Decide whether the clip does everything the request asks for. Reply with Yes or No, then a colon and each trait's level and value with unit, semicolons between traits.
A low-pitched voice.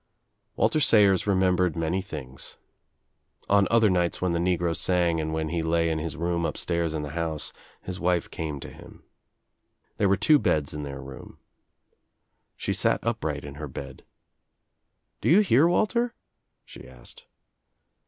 Yes: very low, 85 Hz